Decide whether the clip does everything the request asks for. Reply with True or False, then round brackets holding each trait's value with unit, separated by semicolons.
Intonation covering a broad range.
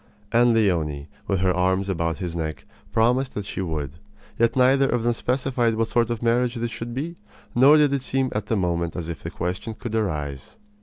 True (5.8 semitones)